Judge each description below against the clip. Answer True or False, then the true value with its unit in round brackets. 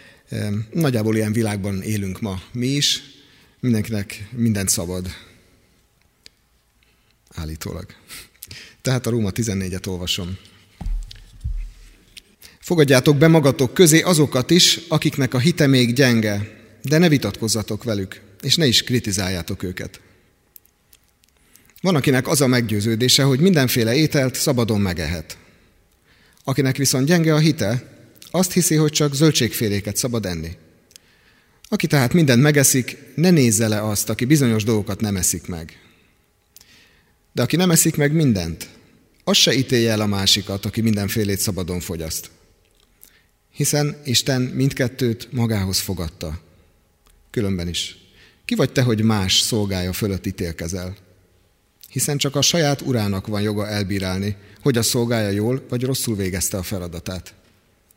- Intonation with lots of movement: True (5.9 semitones)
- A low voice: True (110 Hz)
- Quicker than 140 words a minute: False (125 wpm)